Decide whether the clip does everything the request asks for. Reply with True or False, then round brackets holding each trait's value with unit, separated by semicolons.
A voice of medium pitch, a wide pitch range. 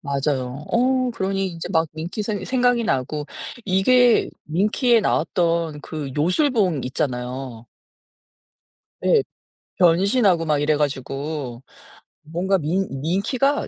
True (170 Hz; 6.0 semitones)